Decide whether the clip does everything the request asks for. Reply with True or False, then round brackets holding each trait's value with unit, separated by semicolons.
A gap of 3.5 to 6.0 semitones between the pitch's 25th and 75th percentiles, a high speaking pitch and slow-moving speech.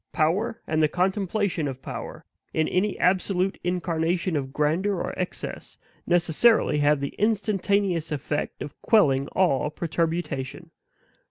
False (4.2 semitones; 175 Hz; 120 wpm)